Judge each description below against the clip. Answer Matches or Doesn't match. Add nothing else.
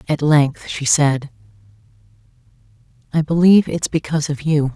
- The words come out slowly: Matches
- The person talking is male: Doesn't match